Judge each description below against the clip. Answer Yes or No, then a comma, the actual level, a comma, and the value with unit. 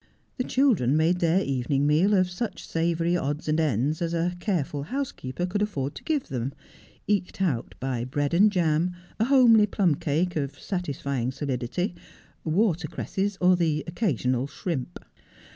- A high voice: No, medium, 165 Hz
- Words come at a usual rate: Yes, average, 160 wpm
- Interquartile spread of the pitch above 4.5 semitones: Yes, average, 5.1 semitones